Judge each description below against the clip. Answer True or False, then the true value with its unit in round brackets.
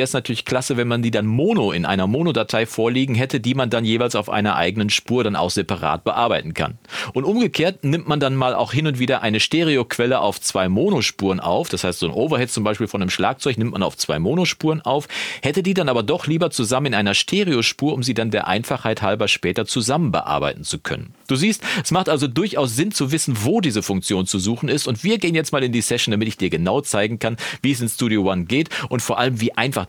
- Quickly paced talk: True (240 wpm)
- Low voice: True (125 Hz)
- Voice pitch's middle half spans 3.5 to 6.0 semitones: True (5.1 semitones)